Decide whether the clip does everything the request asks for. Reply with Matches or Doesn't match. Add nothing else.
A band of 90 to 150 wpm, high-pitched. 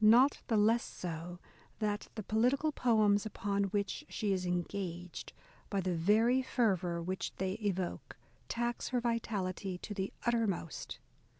Matches